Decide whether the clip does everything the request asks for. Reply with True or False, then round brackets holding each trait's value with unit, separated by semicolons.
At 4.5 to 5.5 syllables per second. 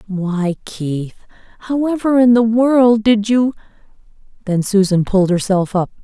False (4.3 syllables/s)